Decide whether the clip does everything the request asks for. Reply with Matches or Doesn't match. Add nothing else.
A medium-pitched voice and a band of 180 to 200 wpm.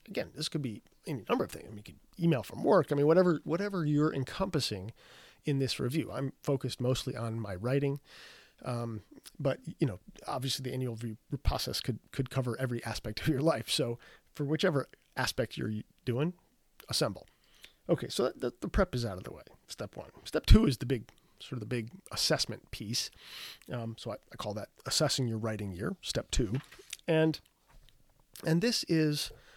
Doesn't match